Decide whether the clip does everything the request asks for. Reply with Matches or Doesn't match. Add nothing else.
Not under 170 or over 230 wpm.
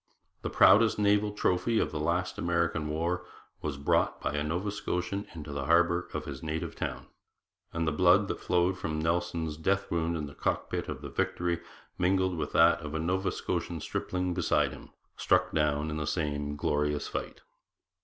Matches